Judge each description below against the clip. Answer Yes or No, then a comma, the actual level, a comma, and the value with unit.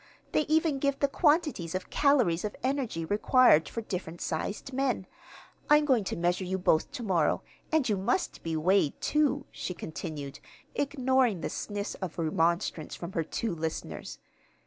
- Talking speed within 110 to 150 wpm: No, average, 160 wpm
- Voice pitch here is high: Yes, high, 200 Hz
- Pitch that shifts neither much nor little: No, wide, 8.2 semitones